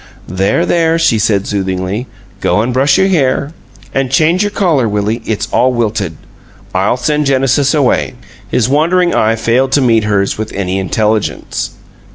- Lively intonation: Yes, wide, 5.8 semitones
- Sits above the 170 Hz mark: No, low, 120 Hz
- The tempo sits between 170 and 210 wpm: No, average, 160 wpm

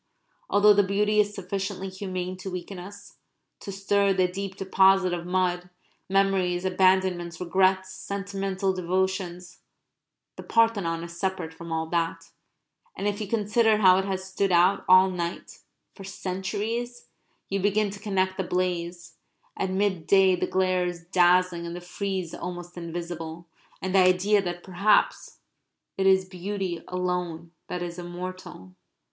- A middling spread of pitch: No, narrow, 1.8 semitones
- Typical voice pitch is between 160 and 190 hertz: Yes, medium, 185 Hz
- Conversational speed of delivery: Yes, average, 145 wpm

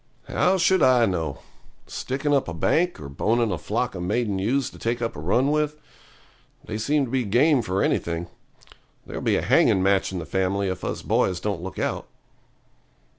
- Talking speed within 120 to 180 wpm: No, average, 190 wpm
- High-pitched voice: No, low, 110 Hz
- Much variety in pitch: Yes, wide, 6.2 semitones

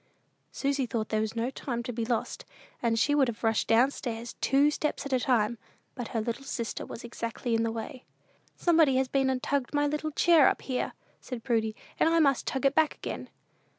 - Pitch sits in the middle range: No, very high, 250 Hz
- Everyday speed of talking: No, fast, 220 wpm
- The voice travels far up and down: No, average, 3.5 semitones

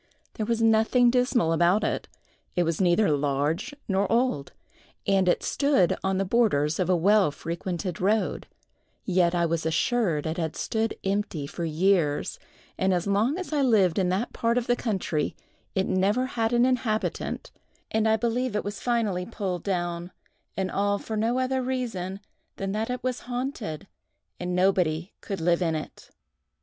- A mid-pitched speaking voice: No, high, 195 Hz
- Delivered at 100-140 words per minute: No, average, 165 wpm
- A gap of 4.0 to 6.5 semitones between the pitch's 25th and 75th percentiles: Yes, average, 4.9 semitones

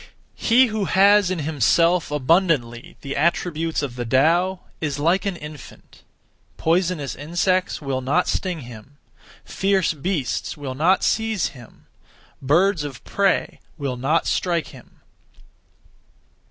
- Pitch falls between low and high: Yes, medium, 160 Hz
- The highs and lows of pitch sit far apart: No, average, 5.0 semitones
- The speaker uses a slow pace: Yes, slow, 125 wpm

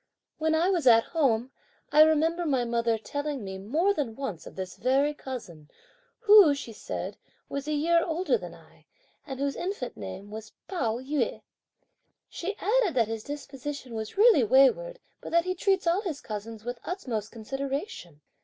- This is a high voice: Yes, very high, 275 Hz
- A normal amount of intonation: No, wide, 6.8 semitones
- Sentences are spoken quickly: No, average, 175 wpm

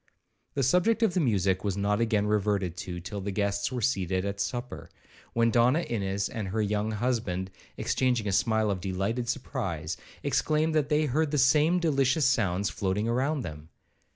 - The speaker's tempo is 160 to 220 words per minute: Yes, average, 170 wpm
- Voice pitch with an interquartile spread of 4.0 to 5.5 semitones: Yes, average, 5.2 semitones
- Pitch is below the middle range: Yes, low, 110 Hz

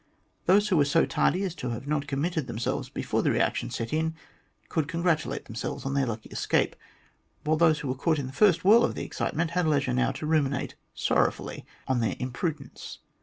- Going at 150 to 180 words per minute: No, average, 200 wpm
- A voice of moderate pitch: Yes, medium, 150 Hz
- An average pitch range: Yes, average, 4.1 semitones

